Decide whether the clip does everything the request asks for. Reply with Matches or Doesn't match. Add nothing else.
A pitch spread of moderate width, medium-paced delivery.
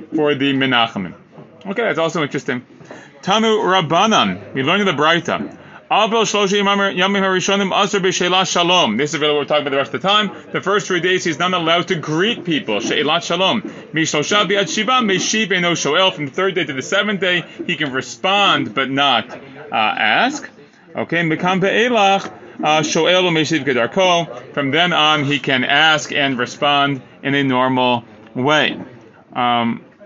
Doesn't match